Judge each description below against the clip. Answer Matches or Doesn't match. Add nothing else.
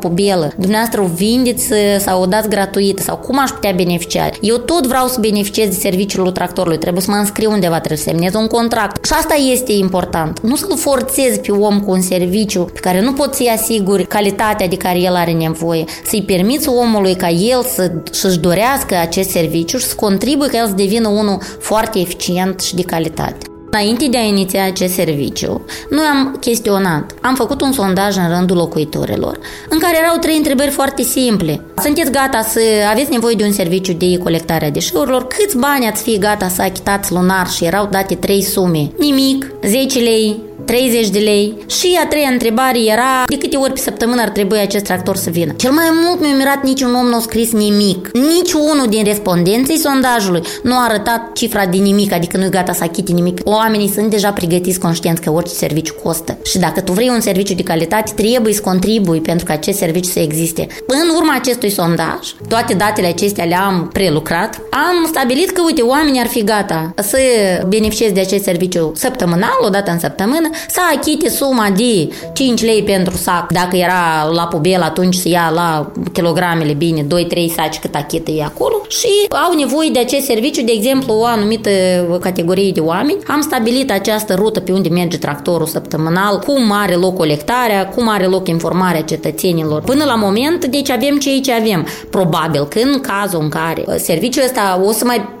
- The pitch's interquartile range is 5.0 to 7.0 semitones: Matches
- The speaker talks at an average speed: Doesn't match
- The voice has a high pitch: Matches